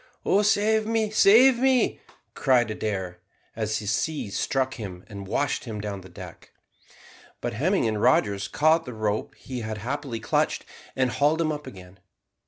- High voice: No, low, 120 Hz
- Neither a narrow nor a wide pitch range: No, wide, 7.3 semitones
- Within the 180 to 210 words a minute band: No, average, 165 wpm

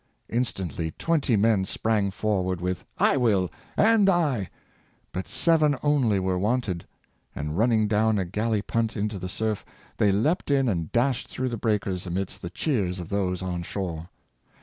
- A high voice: No, low, 105 Hz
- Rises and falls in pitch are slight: No, average, 4.4 semitones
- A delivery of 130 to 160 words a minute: No, average, 170 wpm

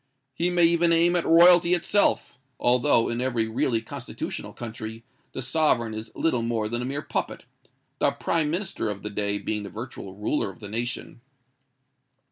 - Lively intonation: Yes, wide, 6.8 semitones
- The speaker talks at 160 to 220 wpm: Yes, average, 165 wpm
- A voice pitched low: Yes, low, 120 Hz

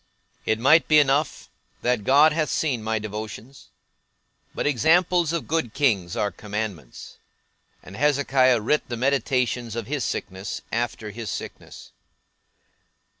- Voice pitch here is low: Yes, low, 125 Hz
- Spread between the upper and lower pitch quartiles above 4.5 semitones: Yes, average, 5.1 semitones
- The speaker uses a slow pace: Yes, slow, 125 wpm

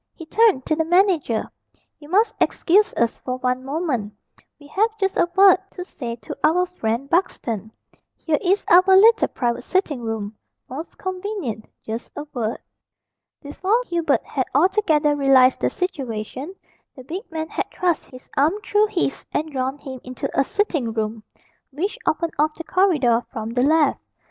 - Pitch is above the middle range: Yes, very high, 300 Hz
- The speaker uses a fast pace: No, average, 165 wpm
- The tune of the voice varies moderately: No, wide, 6.4 semitones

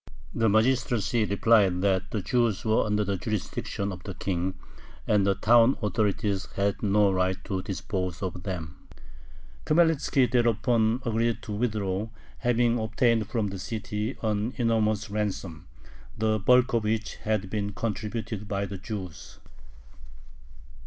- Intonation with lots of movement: No, average, 2.7 semitones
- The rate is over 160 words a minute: No, slow, 135 wpm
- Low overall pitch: Yes, low, 105 Hz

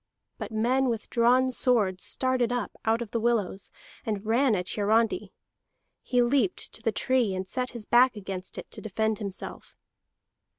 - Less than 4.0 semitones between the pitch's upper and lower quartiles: Yes, average, 3.1 semitones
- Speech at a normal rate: Yes, average, 165 wpm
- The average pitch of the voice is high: Yes, high, 230 Hz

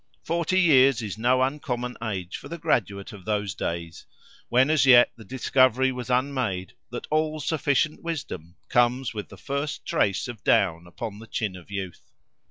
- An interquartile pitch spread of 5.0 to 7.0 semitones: Yes, wide, 5.5 semitones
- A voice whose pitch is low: Yes, low, 120 Hz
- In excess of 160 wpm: Yes, average, 170 wpm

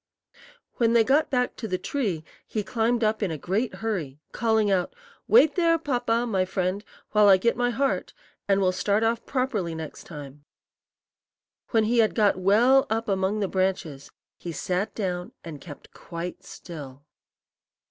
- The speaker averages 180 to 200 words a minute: No, average, 165 wpm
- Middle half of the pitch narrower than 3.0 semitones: No, average, 4.5 semitones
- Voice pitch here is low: No, high, 205 Hz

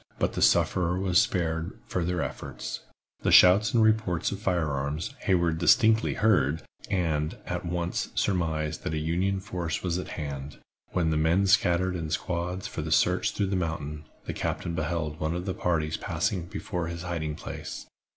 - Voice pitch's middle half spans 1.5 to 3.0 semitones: Yes, average, 2.7 semitones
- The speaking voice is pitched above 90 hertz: No, very low, 85 Hz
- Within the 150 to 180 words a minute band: Yes, average, 170 wpm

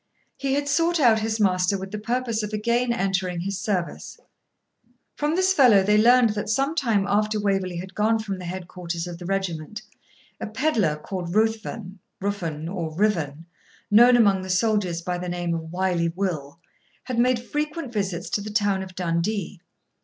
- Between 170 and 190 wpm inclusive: Yes, average, 175 wpm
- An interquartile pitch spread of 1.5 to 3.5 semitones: No, average, 4.0 semitones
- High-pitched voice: Yes, high, 200 Hz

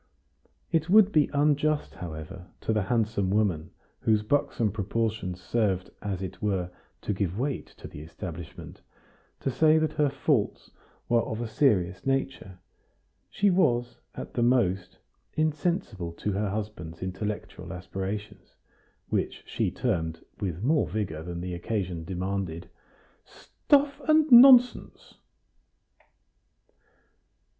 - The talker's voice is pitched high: No, low, 105 Hz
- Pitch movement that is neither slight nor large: No, wide, 6.9 semitones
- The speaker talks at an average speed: No, slow, 120 wpm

